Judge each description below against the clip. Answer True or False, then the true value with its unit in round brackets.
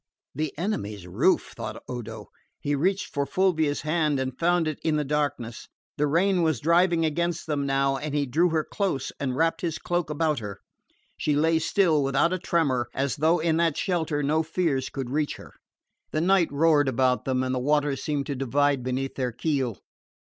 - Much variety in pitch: False (3.5 semitones)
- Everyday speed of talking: True (190 wpm)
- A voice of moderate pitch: True (150 Hz)